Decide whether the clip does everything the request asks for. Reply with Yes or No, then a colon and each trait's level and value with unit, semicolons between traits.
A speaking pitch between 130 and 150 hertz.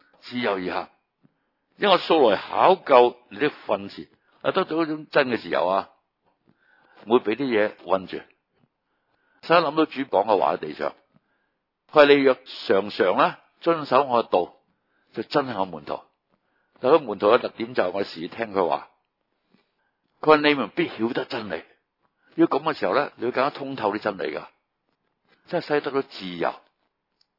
Yes: medium, 140 Hz